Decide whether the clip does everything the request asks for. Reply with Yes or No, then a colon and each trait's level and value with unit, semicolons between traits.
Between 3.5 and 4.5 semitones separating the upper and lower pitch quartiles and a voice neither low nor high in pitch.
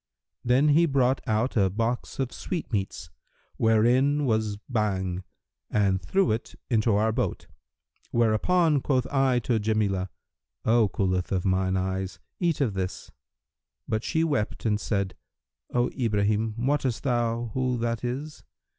No: average, 4.2 semitones; low, 115 Hz